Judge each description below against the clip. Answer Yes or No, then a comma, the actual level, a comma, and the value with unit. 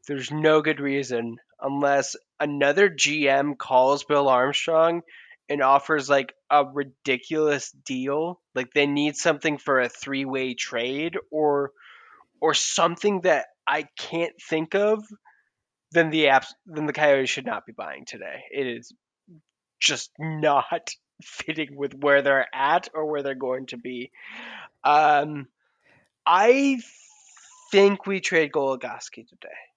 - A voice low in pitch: No, medium, 145 Hz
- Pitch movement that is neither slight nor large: Yes, average, 3.1 semitones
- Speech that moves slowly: Yes, slow, 130 wpm